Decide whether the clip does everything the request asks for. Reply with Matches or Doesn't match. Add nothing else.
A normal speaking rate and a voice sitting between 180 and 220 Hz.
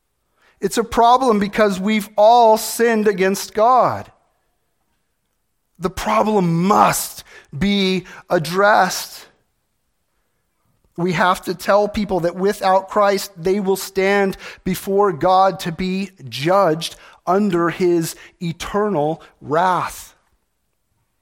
Doesn't match